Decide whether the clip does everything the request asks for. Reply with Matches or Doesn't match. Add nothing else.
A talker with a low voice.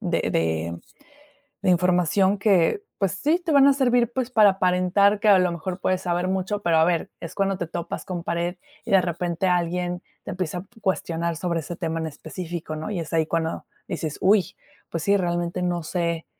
Doesn't match